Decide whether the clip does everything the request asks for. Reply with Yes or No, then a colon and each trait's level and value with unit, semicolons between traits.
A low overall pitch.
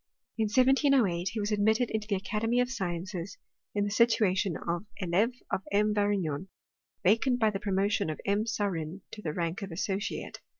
No: high, 205 Hz